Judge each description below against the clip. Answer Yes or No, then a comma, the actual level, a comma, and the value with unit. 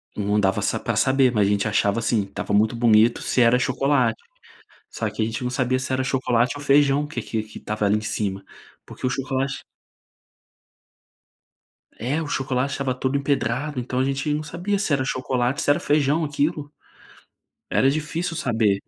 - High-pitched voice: No, low, 130 Hz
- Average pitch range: Yes, average, 4.1 semitones